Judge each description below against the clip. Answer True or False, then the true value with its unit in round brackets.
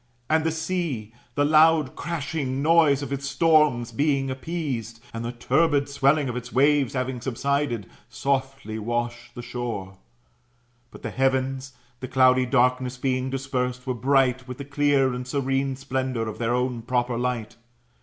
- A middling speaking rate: True (155 wpm)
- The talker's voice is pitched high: False (130 Hz)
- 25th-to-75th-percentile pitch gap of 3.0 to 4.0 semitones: False (2.4 semitones)